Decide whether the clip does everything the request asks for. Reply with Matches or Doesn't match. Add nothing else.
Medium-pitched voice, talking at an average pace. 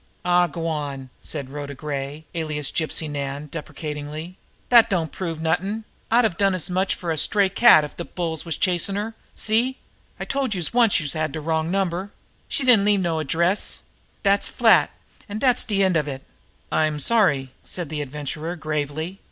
Matches